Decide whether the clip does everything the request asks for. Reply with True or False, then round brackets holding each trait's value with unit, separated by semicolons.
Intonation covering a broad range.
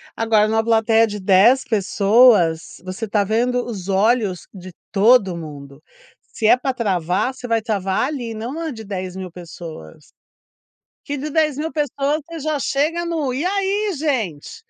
True (6.4 semitones)